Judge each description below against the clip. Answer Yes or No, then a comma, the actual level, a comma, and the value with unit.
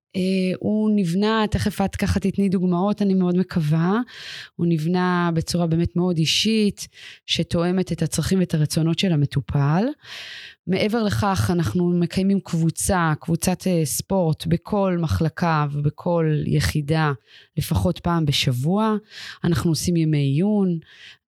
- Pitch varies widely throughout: No, average, 2.8 semitones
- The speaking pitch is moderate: Yes, medium, 175 Hz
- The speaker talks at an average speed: Yes, average, 120 wpm